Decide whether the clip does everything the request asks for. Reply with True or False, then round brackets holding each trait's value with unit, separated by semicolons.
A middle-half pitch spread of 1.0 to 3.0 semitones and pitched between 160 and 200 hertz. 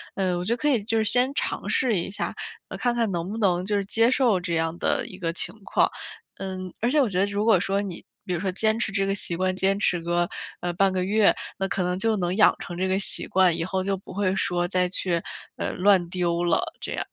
True (2.6 semitones; 190 Hz)